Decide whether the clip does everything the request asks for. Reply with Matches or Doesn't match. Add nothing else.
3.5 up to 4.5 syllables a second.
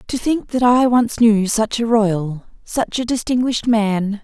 Matches